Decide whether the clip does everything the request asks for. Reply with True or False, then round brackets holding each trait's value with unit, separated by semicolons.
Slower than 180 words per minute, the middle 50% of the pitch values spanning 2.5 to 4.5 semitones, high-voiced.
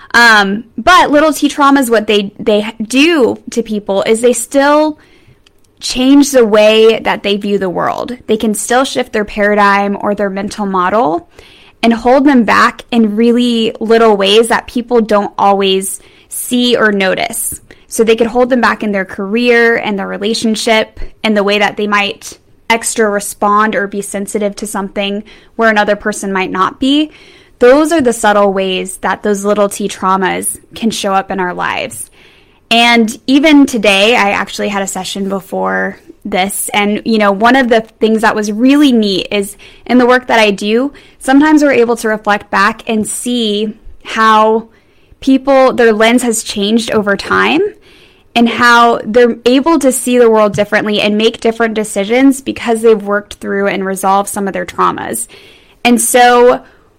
True (170 wpm; 3.1 semitones; 220 Hz)